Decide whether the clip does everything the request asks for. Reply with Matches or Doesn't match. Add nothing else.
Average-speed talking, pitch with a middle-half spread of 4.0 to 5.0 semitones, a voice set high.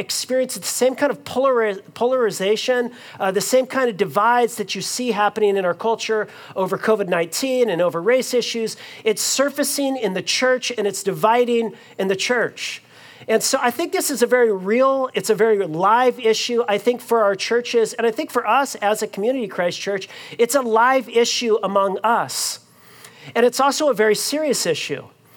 Doesn't match